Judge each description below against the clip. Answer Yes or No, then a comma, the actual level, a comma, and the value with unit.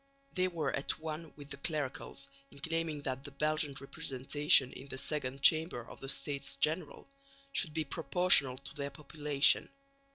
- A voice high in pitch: No, medium, 145 Hz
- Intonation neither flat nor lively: No, narrow, 2.3 semitones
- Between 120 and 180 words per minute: Yes, average, 160 wpm